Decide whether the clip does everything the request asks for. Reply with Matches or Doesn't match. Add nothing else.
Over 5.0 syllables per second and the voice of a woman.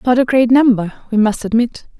Matches